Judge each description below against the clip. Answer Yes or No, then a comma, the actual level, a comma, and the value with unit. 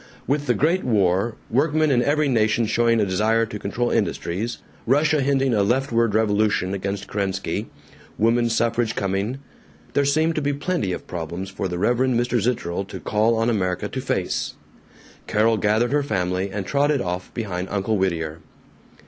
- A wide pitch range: No, average, 4.6 semitones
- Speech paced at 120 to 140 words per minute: No, average, 165 wpm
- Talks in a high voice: No, low, 110 Hz